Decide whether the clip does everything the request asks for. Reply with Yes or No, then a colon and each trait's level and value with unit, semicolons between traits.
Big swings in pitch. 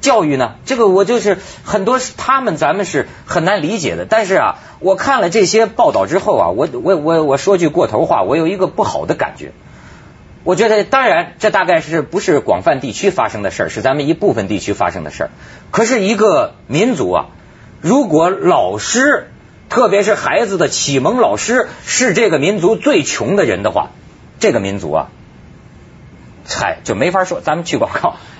No: average, 4.7 semitones